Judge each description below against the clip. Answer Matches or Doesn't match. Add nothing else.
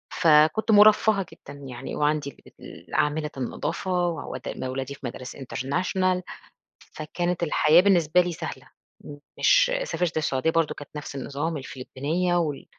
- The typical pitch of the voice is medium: Matches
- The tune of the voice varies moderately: Matches